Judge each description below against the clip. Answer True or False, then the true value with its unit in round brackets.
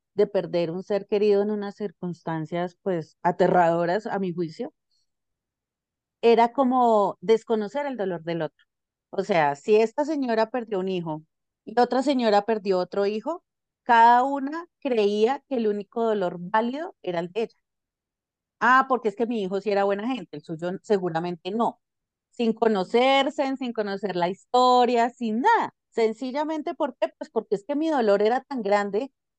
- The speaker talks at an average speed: True (165 wpm)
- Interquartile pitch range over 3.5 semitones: True (5.0 semitones)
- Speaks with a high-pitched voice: True (215 Hz)